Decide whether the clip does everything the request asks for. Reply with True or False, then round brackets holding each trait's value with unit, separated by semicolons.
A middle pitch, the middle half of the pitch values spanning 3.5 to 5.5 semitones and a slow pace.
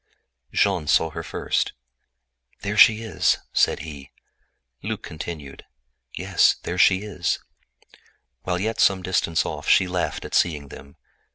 False (90 Hz; 4.0 semitones; 130 wpm)